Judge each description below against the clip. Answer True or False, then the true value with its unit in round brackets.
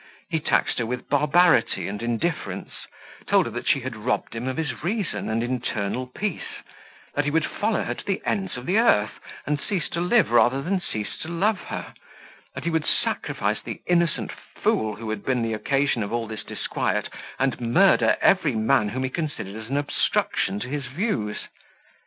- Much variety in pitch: True (6.9 semitones)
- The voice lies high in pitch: False (135 Hz)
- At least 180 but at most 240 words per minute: True (190 wpm)